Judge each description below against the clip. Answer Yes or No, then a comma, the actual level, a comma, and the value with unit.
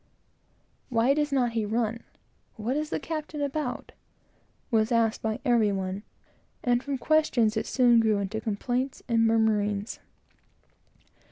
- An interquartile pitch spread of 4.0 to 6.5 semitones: No, average, 3.4 semitones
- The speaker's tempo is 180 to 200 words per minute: No, slow, 135 wpm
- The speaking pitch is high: Yes, high, 230 Hz